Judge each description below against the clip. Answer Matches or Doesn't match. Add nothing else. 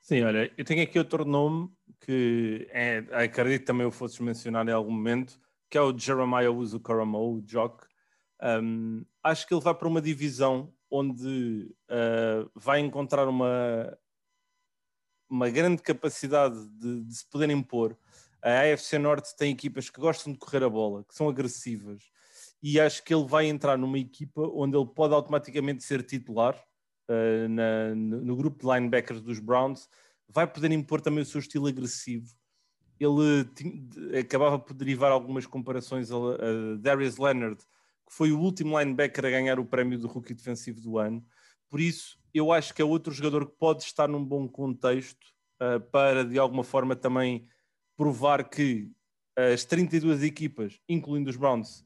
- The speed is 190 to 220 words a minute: Doesn't match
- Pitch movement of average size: Matches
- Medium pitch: Doesn't match